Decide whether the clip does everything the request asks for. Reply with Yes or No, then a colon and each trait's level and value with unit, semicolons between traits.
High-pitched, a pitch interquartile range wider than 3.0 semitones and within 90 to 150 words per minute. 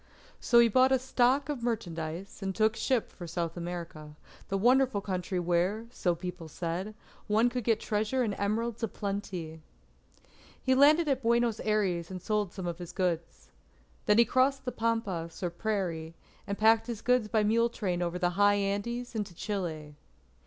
No: high, 205 Hz; average, 4.9 semitones; average, 175 wpm